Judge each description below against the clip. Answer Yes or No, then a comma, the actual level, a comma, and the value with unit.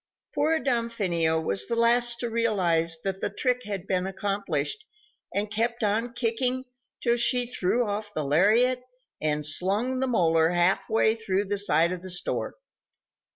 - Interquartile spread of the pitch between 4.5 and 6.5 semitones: Yes, average, 4.9 semitones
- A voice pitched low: No, high, 205 Hz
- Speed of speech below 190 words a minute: Yes, average, 155 wpm